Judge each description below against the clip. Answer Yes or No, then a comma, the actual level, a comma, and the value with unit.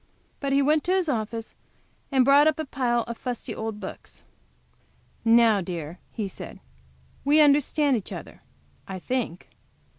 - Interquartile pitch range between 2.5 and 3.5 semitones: No, average, 4.6 semitones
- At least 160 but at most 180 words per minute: No, average, 150 wpm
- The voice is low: No, high, 245 Hz